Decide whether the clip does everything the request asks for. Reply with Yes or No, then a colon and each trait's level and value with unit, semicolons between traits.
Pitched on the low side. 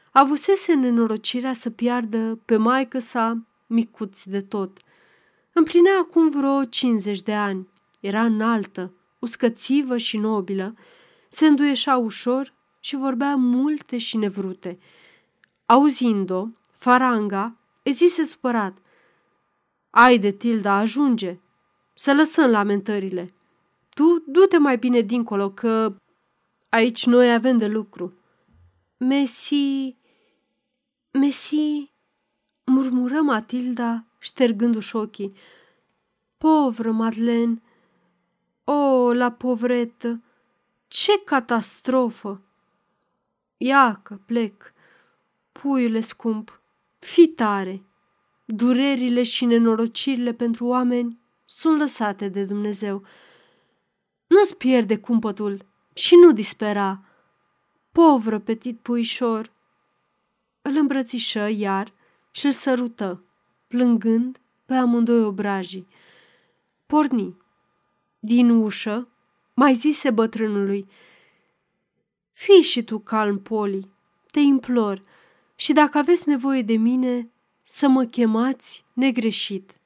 No: high, 235 Hz